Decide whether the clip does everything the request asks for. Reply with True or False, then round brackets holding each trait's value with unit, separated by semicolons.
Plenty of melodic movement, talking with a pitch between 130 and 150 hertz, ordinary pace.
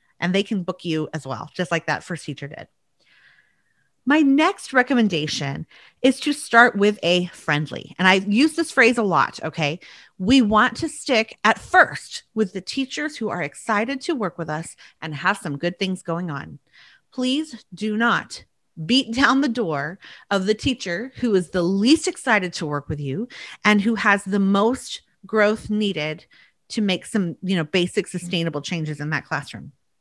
False (6.3 semitones; 195 Hz; 180 wpm)